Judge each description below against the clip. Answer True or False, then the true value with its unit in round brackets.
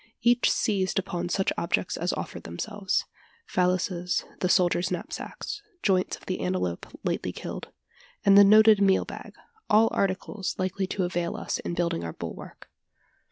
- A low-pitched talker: False (185 Hz)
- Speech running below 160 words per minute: True (150 wpm)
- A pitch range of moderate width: False (2.1 semitones)